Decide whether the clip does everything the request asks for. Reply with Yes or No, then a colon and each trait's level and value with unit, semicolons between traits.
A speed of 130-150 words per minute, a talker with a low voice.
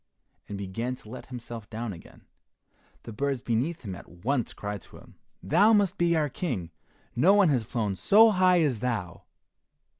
No: average, 175 wpm; low, 125 Hz